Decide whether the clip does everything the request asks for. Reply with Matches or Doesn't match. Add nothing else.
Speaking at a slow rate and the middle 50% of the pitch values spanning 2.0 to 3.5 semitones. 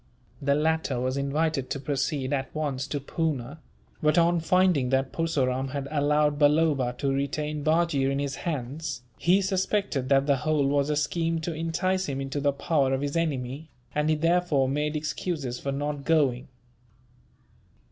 Doesn't match